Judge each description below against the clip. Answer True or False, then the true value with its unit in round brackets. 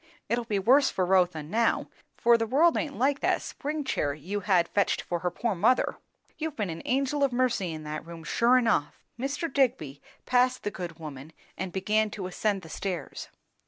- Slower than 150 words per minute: False (195 wpm)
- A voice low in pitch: False (210 Hz)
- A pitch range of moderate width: False (6.6 semitones)